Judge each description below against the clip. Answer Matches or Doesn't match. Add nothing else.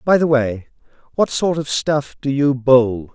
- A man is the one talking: Matches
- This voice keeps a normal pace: Matches